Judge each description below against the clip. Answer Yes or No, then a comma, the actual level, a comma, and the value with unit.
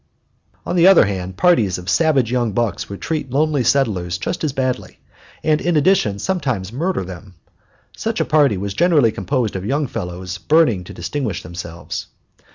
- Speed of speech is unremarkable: Yes, average, 165 wpm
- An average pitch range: No, wide, 8.3 semitones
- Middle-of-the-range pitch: No, low, 120 Hz